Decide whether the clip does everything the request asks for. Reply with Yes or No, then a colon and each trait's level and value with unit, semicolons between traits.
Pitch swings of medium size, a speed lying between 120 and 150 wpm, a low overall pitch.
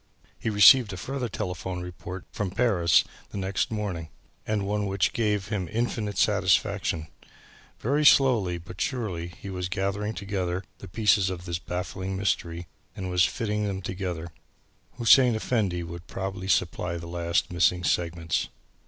Yes: average, 3.1 semitones; average, 145 wpm; very low, 95 Hz